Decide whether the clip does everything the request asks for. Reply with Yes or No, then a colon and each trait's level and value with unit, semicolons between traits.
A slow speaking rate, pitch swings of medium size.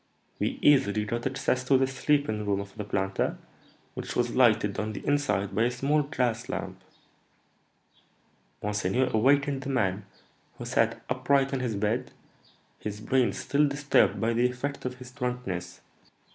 No: average, 155 wpm; average, 4.3 semitones